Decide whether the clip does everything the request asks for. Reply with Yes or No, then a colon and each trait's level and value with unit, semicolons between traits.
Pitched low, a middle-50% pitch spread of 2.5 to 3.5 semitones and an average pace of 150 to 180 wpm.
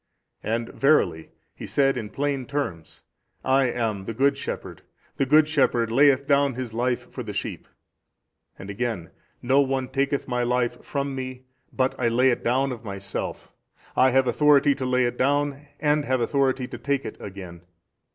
Yes: low, 130 Hz; average, 2.8 semitones; average, 170 wpm